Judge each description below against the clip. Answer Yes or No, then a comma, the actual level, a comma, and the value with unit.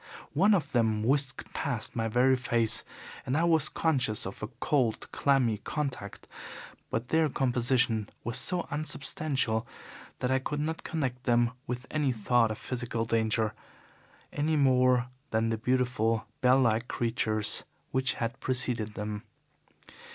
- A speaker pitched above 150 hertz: No, low, 125 Hz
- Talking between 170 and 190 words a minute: No, average, 140 wpm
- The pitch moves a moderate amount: Yes, average, 3.1 semitones